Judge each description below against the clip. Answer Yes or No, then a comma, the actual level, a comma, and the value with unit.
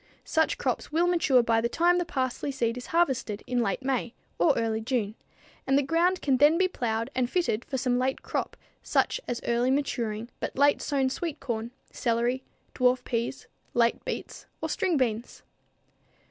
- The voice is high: Yes, very high, 255 Hz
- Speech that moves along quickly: No, average, 175 wpm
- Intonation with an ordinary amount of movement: Yes, average, 3.8 semitones